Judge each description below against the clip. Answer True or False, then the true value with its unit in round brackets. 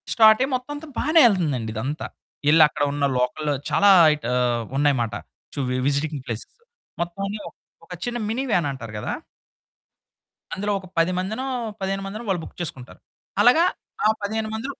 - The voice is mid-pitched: True (175 Hz)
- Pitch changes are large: True (7.5 semitones)